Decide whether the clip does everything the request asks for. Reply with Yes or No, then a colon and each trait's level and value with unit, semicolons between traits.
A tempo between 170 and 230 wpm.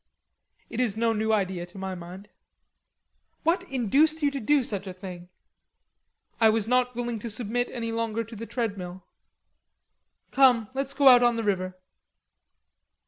No: average, 155 wpm